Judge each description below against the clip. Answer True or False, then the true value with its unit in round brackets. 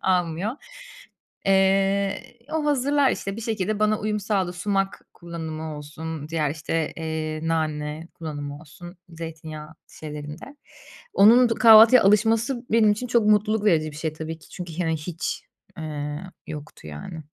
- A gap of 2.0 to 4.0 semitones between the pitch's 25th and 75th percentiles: False (5.3 semitones)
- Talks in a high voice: False (175 Hz)